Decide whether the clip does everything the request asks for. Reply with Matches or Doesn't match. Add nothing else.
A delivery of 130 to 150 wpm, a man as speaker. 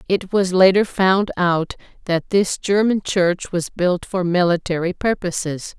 Doesn't match